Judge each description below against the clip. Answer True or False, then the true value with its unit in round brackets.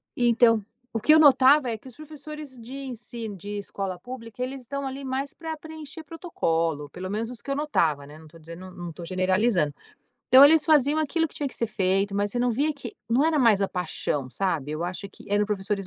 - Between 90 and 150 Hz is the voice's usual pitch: False (230 Hz)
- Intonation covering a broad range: True (7.0 semitones)